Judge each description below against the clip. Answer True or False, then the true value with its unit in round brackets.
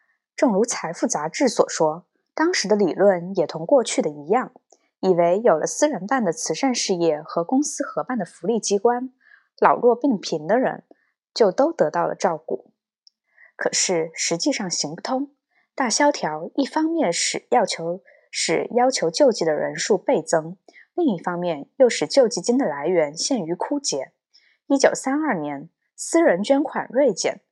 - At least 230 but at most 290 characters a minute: True (240 characters per minute)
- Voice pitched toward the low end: False (240 Hz)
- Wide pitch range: True (8.1 semitones)